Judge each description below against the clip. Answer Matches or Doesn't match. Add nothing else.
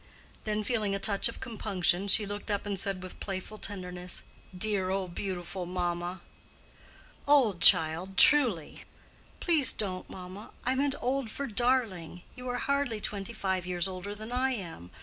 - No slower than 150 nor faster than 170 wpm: Matches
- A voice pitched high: Matches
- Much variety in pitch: Doesn't match